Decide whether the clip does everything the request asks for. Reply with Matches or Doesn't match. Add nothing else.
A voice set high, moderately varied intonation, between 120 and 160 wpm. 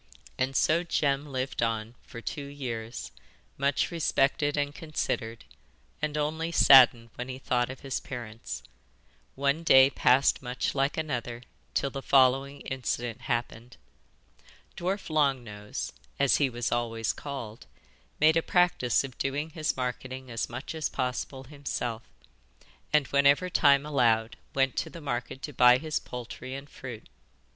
Doesn't match